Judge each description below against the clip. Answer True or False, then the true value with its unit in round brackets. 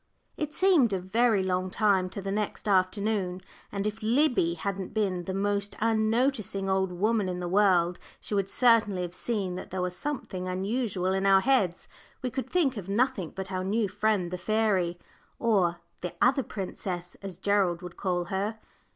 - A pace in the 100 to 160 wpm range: False (175 wpm)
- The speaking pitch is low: False (195 Hz)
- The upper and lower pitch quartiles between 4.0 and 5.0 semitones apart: False (3.1 semitones)